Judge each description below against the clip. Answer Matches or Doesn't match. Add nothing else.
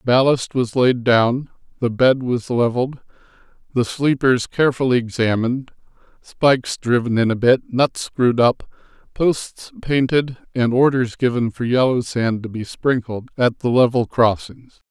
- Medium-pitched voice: Doesn't match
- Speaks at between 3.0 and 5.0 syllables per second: Matches